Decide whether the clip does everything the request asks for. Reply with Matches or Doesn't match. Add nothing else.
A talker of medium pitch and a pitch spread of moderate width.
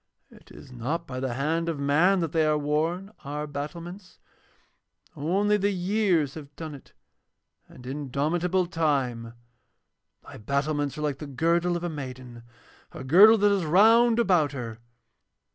Matches